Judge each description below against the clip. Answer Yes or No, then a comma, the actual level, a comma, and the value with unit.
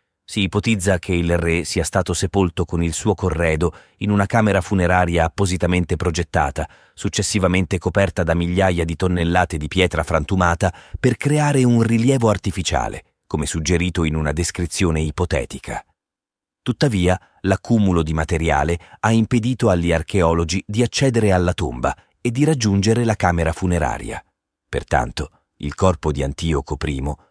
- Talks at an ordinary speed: Yes, average, 135 wpm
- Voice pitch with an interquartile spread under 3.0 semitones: No, average, 3.3 semitones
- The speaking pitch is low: Yes, very low, 90 Hz